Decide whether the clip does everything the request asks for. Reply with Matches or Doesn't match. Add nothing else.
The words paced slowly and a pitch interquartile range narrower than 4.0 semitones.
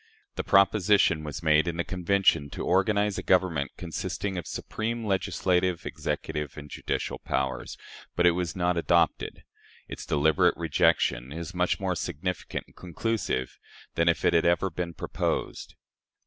Doesn't match